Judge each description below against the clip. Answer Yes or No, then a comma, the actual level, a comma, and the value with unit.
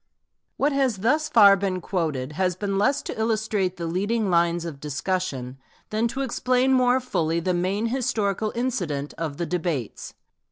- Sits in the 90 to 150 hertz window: No, high, 195 Hz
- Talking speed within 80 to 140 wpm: No, average, 160 wpm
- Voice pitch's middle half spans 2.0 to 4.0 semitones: No, wide, 5.6 semitones